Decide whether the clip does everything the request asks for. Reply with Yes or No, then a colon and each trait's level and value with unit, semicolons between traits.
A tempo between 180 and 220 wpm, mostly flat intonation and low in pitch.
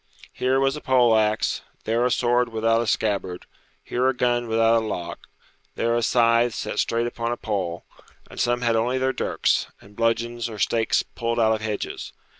Yes: average, 190 wpm; narrow, 1.6 semitones; low, 115 Hz